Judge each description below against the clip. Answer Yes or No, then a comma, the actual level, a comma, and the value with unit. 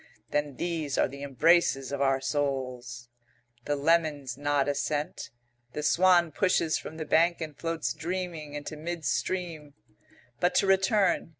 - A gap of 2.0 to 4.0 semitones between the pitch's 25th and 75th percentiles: Yes, average, 3.3 semitones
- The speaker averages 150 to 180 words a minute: No, average, 140 wpm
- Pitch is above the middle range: No, medium, 150 Hz